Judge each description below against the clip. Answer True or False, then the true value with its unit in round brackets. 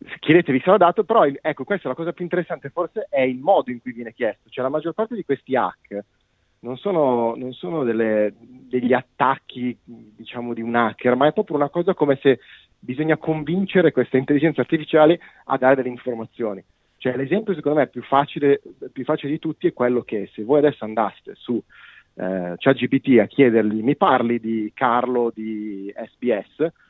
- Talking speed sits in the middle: False (185 wpm)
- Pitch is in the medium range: False (130 Hz)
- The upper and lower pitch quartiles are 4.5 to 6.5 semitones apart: True (4.8 semitones)